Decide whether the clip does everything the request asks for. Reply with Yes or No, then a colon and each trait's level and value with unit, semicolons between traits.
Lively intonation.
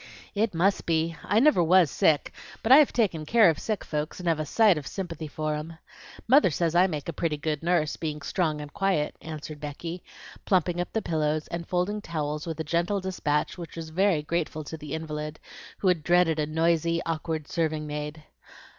No: average, 2.8 semitones